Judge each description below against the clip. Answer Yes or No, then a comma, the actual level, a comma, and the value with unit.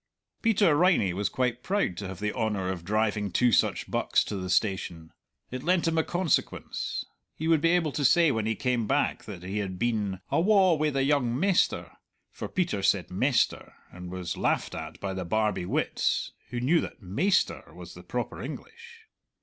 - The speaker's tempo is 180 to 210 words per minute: Yes, average, 190 wpm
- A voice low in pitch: Yes, low, 120 Hz